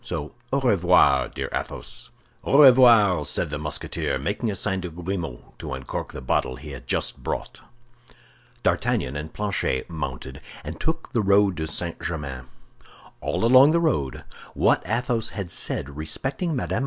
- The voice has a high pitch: No, very low, 90 Hz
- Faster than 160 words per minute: No, average, 155 wpm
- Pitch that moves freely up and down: Yes, wide, 8.0 semitones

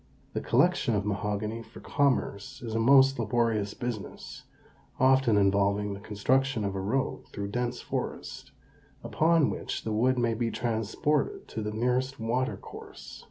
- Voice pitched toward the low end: Yes, low, 115 Hz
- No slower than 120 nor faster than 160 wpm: Yes, average, 155 wpm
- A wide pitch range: No, average, 3.8 semitones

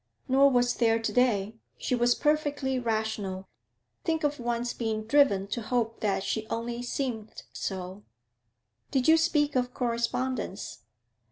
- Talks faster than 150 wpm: No, average, 140 wpm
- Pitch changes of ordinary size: Yes, average, 3.3 semitones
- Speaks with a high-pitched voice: Yes, high, 240 Hz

